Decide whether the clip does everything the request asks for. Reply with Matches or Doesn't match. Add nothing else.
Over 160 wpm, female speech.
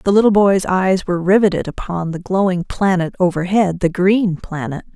Matches